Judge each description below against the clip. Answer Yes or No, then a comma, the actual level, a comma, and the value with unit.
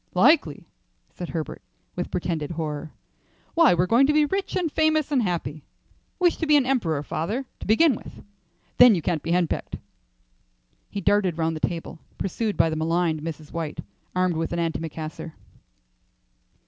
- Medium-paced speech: Yes, average, 160 wpm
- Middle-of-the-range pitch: Yes, medium, 175 Hz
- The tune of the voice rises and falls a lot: Yes, wide, 7.9 semitones